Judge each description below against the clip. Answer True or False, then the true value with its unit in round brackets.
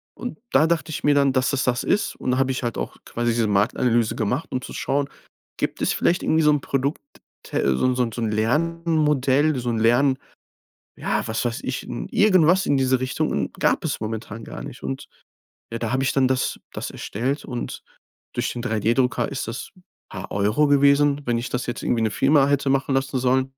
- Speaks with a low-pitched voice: True (130 Hz)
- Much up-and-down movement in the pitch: False (3.5 semitones)